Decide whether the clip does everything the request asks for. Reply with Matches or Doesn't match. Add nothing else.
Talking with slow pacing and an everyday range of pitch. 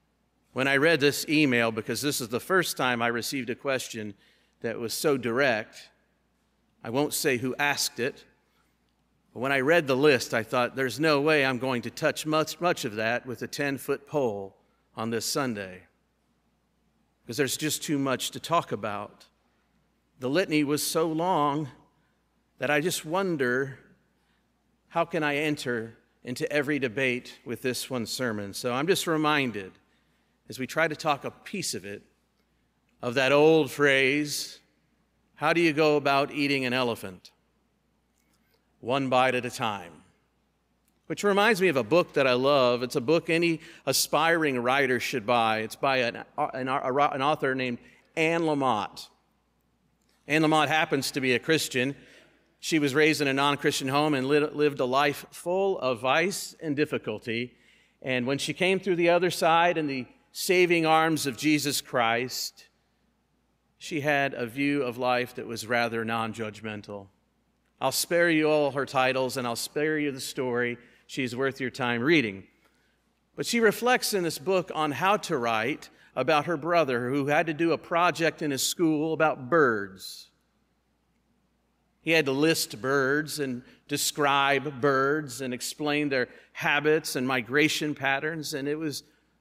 Doesn't match